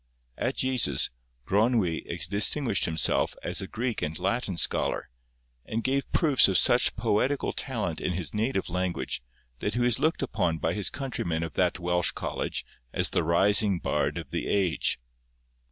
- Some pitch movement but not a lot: No, wide, 5.7 semitones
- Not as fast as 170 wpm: Yes, average, 155 wpm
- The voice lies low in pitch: Yes, low, 100 Hz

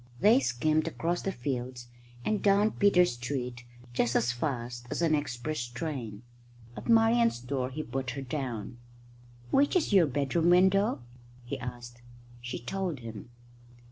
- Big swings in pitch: Yes, wide, 6.6 semitones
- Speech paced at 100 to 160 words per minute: Yes, average, 140 wpm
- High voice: No, low, 135 Hz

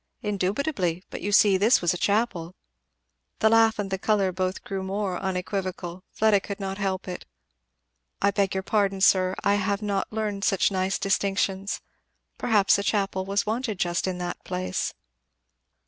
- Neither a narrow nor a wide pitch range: No, narrow, 1.7 semitones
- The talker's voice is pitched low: No, high, 195 Hz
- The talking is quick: No, average, 165 wpm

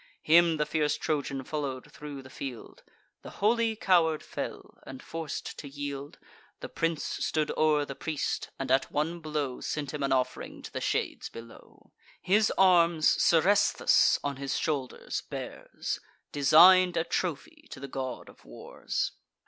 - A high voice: No, medium, 150 Hz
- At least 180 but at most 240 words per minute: No, average, 150 wpm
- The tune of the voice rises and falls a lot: No, average, 3.4 semitones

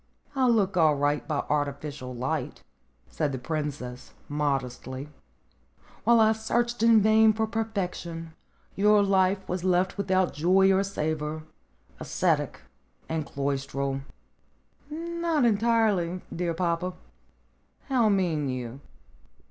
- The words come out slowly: Yes, slow, 110 wpm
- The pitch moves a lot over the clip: Yes, wide, 6.7 semitones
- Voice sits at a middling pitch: Yes, medium, 180 Hz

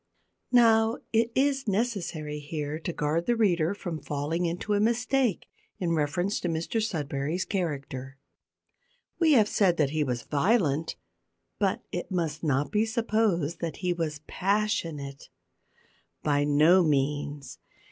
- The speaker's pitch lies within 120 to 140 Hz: No, medium, 170 Hz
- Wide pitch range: Yes, wide, 6.2 semitones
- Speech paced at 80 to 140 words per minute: Yes, slow, 135 wpm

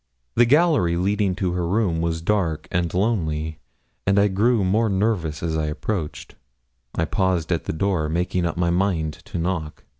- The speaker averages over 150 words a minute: Yes, average, 175 wpm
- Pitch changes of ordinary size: Yes, average, 3.6 semitones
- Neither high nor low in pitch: No, very low, 90 Hz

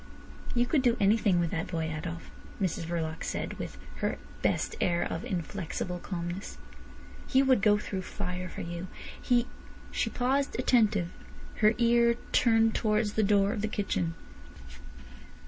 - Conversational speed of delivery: Yes, average, 145 wpm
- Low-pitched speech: No, high, 200 Hz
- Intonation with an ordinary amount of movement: Yes, average, 5.0 semitones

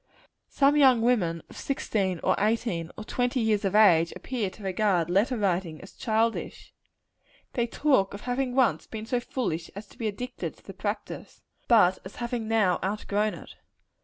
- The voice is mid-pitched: No, high, 215 Hz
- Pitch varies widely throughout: No, average, 4.2 semitones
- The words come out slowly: No, average, 170 wpm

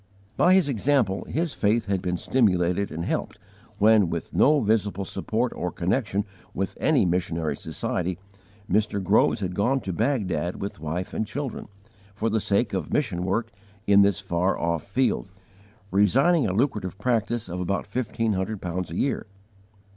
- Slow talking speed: No, average, 160 wpm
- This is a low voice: Yes, low, 100 Hz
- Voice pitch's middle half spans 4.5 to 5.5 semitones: No, average, 4.1 semitones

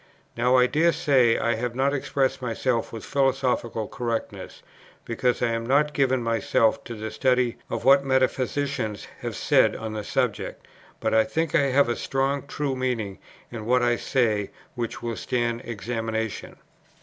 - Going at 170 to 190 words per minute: No, average, 160 wpm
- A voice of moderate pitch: No, low, 125 Hz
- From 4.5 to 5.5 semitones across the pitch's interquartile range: No, average, 2.7 semitones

